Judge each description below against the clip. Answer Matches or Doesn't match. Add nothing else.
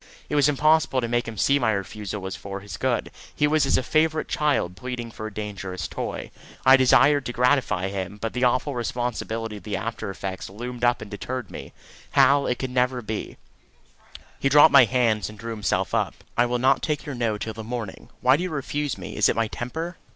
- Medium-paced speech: Doesn't match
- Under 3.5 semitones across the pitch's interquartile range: Doesn't match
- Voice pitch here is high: Doesn't match